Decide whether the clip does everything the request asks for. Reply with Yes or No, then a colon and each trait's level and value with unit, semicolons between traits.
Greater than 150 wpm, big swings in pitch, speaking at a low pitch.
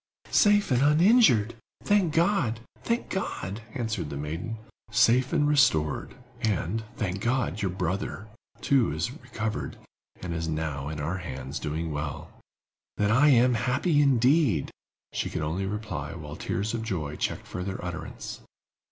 No: average, 140 wpm; wide, 7.9 semitones; low, 110 Hz